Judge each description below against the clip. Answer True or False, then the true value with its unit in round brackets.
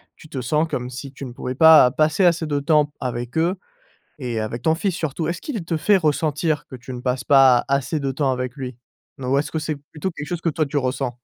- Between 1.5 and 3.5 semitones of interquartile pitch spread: False (3.9 semitones)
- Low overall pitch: False (145 Hz)